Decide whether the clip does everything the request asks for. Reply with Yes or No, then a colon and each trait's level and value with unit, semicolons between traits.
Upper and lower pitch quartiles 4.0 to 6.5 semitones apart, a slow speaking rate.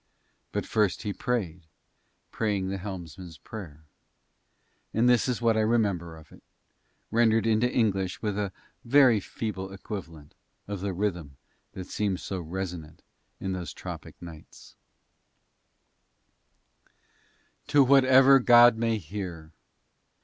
Yes: average, 4.4 semitones; slow, 120 wpm